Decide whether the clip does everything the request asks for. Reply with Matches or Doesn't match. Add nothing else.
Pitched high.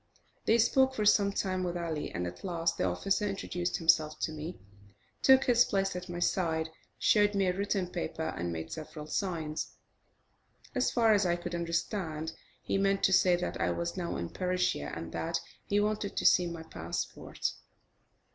Doesn't match